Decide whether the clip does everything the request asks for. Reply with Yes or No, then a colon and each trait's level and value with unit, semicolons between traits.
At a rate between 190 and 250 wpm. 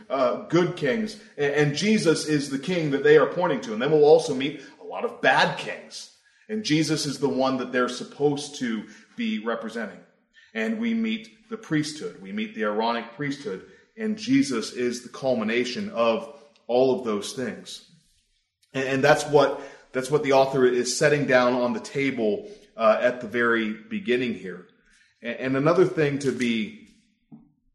No: average, 180 wpm